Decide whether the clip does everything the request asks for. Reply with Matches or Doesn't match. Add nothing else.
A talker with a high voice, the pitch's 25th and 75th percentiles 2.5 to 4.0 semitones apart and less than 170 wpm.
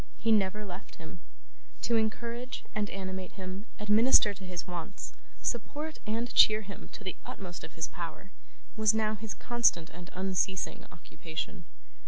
Matches